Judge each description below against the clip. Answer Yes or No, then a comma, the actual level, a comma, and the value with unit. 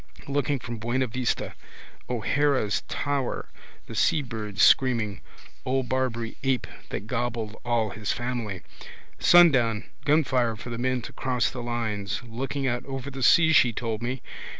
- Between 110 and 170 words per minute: Yes, average, 140 wpm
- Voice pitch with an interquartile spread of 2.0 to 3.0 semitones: Yes, narrow, 2.6 semitones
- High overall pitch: No, low, 120 Hz